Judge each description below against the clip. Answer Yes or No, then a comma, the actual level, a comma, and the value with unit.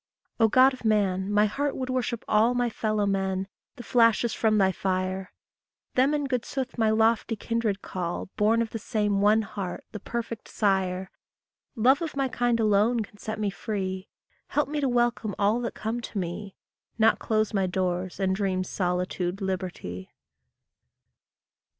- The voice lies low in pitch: No, high, 215 Hz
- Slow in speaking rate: No, average, 165 wpm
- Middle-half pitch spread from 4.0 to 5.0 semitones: No, average, 3.6 semitones